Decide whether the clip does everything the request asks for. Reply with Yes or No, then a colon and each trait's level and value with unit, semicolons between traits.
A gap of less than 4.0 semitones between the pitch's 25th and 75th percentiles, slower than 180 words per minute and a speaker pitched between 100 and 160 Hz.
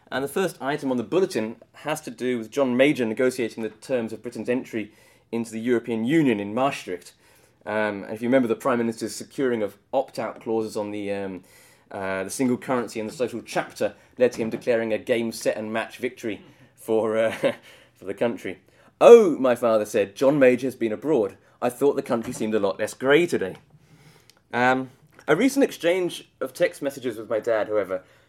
No: average, 3.5 semitones; average, 200 wpm; low, 120 Hz